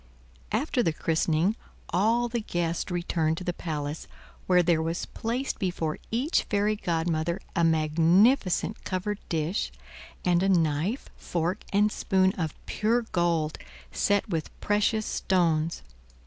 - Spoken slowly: Yes, slow, 130 wpm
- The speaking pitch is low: No, medium, 175 Hz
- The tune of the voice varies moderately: Yes, average, 4.2 semitones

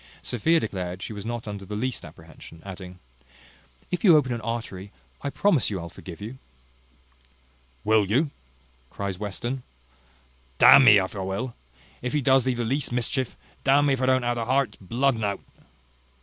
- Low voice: Yes, low, 115 Hz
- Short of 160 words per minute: No, average, 185 wpm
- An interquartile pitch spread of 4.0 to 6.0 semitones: Yes, average, 4.8 semitones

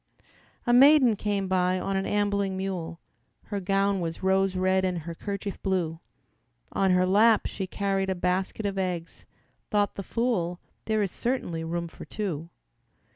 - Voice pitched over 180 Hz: Yes, high, 190 Hz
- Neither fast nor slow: Yes, average, 160 wpm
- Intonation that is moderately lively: No, narrow, 2.0 semitones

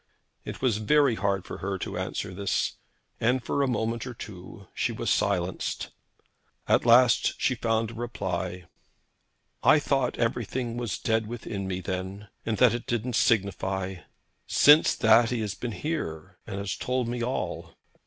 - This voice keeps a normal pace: Yes, average, 165 wpm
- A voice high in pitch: No, low, 110 Hz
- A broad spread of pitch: No, average, 4.0 semitones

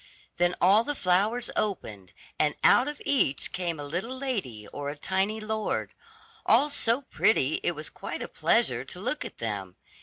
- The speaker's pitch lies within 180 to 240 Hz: Yes, high, 190 Hz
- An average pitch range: No, wide, 8.0 semitones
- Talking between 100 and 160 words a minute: No, average, 175 wpm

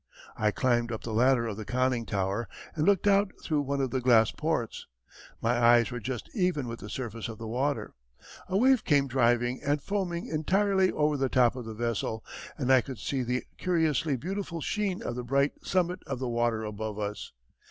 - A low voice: Yes, low, 130 Hz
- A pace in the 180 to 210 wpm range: Yes, average, 200 wpm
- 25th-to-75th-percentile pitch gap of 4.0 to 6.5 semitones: Yes, average, 5.1 semitones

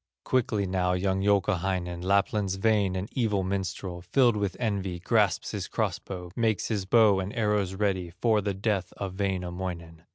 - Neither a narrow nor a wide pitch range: No, narrow, 2.3 semitones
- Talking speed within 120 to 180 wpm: Yes, average, 160 wpm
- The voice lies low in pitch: Yes, very low, 95 Hz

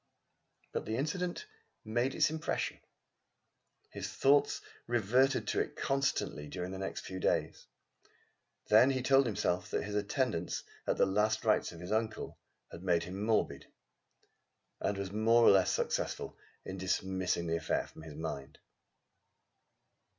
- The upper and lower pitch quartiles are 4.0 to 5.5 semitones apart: Yes, average, 5.1 semitones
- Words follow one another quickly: No, average, 145 wpm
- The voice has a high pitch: No, low, 105 Hz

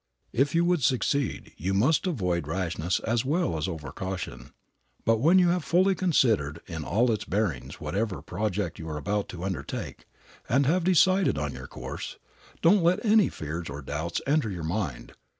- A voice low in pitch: Yes, low, 105 Hz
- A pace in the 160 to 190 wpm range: Yes, average, 175 wpm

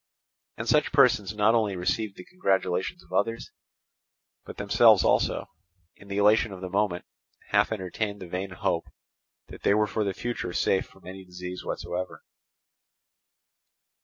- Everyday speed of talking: Yes, average, 150 wpm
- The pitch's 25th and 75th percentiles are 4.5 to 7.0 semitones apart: No, average, 2.9 semitones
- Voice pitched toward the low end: Yes, low, 100 Hz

